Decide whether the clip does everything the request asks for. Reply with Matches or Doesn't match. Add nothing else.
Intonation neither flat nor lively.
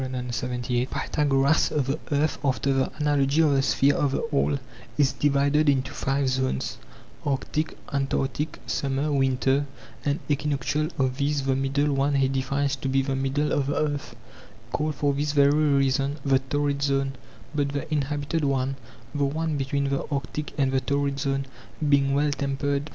Doesn't match